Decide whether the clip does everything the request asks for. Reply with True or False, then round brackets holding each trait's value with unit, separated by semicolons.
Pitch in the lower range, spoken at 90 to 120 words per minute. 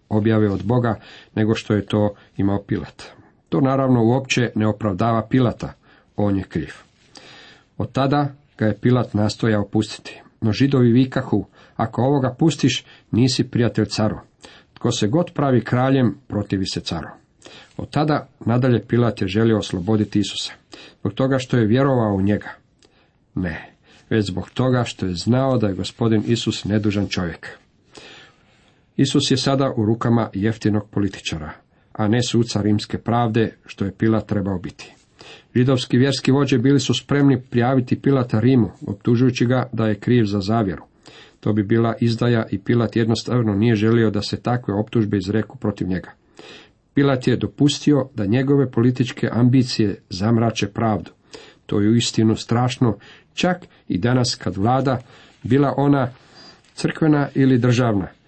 False (115 Hz; 145 wpm)